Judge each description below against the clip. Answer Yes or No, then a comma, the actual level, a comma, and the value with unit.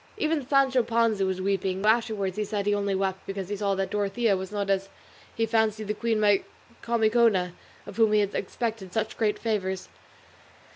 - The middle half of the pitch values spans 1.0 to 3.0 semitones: Yes, narrow, 2.6 semitones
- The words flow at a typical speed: Yes, average, 180 wpm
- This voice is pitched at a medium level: No, high, 210 Hz